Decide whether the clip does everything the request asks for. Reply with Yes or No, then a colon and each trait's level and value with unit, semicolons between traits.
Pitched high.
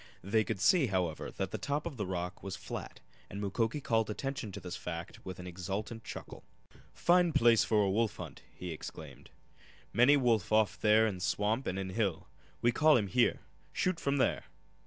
No: low, 110 Hz